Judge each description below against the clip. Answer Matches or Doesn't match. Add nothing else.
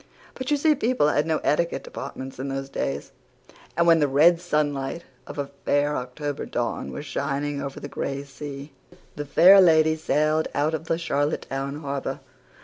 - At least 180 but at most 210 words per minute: Doesn't match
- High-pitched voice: Doesn't match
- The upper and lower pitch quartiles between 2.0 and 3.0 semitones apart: Matches